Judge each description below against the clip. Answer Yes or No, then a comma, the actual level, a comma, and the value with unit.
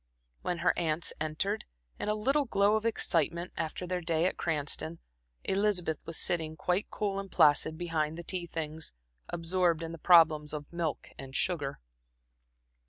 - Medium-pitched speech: Yes, medium, 170 Hz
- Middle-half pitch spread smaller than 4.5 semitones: Yes, average, 2.9 semitones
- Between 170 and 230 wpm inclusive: No, average, 160 wpm